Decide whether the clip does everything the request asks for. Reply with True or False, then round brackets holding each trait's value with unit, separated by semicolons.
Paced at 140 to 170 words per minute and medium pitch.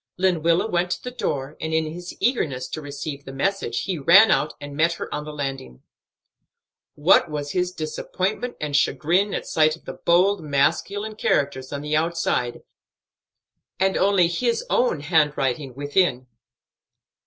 True (155 wpm; 160 Hz)